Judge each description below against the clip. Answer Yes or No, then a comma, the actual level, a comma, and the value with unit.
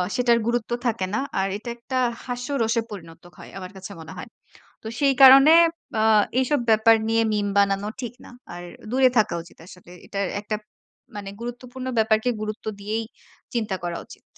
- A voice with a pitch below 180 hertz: No, high, 220 Hz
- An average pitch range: Yes, average, 3.6 semitones